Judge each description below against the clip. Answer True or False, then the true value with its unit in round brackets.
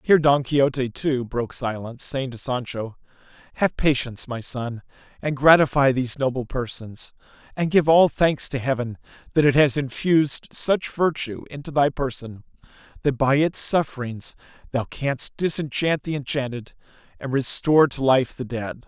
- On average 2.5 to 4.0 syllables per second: False (4.9 syllables/s)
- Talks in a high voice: False (135 Hz)